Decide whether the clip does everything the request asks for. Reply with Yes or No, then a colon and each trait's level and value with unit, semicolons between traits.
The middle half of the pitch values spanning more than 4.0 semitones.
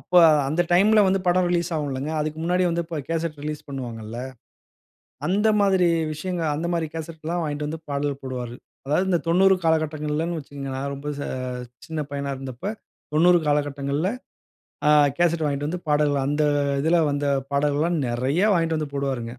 No: average, 3.3 semitones